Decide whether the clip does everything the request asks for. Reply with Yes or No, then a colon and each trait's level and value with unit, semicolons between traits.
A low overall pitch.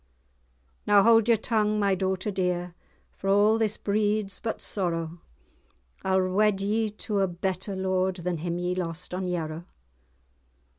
No: high, 190 Hz